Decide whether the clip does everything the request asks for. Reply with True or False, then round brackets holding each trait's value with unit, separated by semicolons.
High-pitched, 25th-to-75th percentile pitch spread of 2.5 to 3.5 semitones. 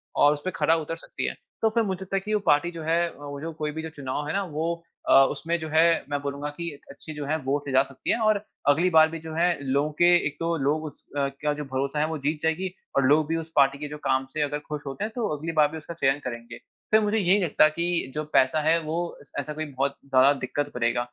False (155 Hz; 2.8 semitones)